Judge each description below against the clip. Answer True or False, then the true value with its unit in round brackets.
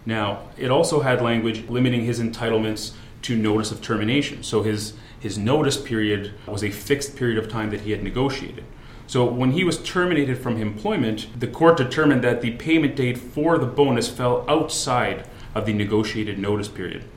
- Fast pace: False (180 wpm)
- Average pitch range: True (3.3 semitones)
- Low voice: True (115 Hz)